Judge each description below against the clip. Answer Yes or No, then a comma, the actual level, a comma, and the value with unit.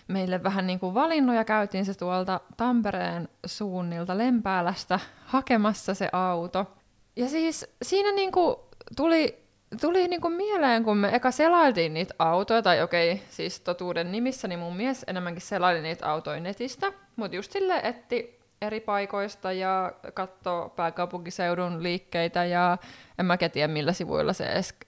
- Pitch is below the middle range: No, high, 190 Hz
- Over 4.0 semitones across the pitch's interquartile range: Yes, wide, 5.5 semitones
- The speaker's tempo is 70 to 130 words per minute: No, average, 140 wpm